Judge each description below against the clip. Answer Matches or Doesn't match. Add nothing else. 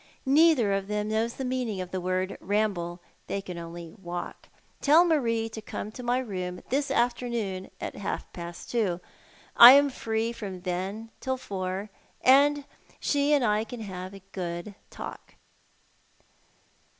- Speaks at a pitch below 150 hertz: Doesn't match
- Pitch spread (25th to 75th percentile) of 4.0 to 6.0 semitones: Matches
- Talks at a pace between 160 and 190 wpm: Doesn't match